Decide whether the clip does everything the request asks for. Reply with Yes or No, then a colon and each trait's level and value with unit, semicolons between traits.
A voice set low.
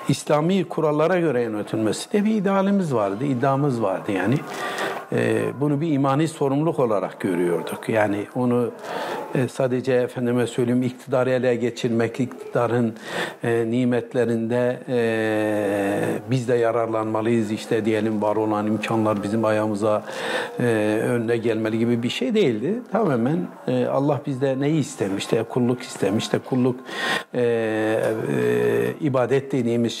Yes: low, 120 Hz